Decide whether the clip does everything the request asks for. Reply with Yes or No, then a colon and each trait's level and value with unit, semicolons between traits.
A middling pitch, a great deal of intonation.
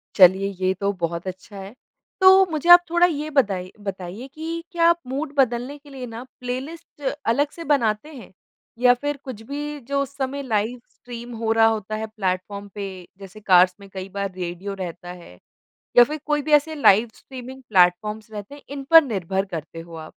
No: high, 230 Hz; wide, 6.5 semitones